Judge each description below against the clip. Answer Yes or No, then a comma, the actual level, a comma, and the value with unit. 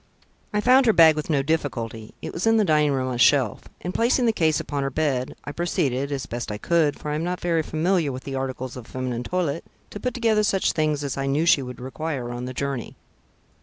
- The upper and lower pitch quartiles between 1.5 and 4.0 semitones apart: No, average, 4.7 semitones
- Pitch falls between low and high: Yes, medium, 145 Hz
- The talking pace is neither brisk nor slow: No, fast, 240 wpm